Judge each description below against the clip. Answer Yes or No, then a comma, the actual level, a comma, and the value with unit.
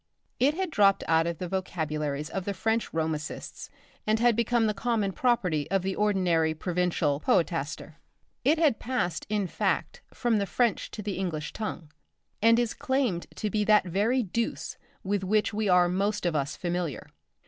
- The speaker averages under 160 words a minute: No, average, 170 wpm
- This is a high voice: Yes, high, 195 Hz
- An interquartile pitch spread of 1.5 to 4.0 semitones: No, average, 4.8 semitones